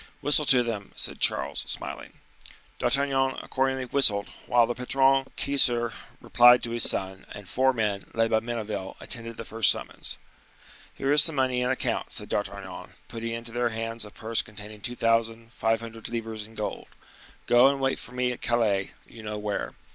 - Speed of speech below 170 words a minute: No, average, 175 wpm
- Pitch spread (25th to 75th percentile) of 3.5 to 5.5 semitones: No, narrow, 2.6 semitones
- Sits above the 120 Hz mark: No, low, 115 Hz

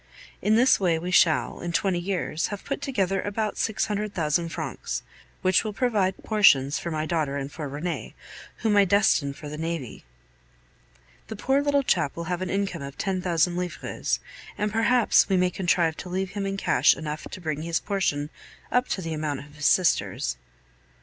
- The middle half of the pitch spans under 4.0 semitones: No, average, 4.4 semitones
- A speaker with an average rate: Yes, average, 190 wpm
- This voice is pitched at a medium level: Yes, medium, 180 Hz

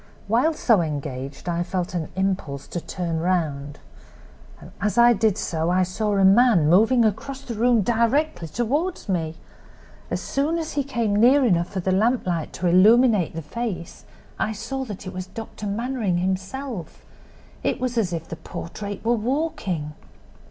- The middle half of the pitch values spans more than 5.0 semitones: Yes, wide, 5.6 semitones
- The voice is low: No, high, 200 Hz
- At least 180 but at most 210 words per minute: No, average, 160 wpm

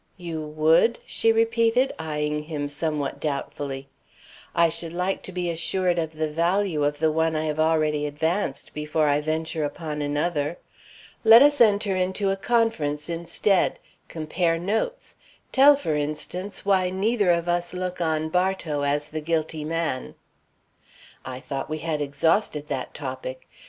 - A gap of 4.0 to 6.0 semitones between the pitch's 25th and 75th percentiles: No, average, 3.6 semitones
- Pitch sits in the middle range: Yes, medium, 160 Hz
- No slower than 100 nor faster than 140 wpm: No, average, 150 wpm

